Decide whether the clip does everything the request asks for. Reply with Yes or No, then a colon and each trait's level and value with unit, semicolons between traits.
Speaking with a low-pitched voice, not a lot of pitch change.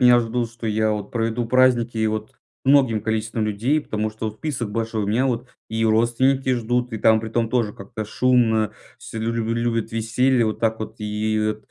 Yes: low, 115 Hz; narrow, 1.9 semitones